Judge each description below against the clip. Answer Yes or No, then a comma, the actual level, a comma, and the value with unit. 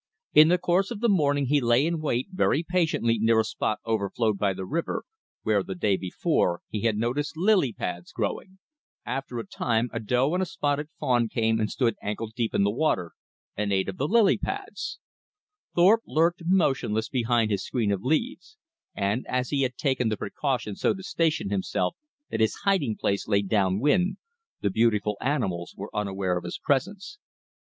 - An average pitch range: No, wide, 7.1 semitones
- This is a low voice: Yes, low, 120 Hz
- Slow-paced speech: No, average, 185 wpm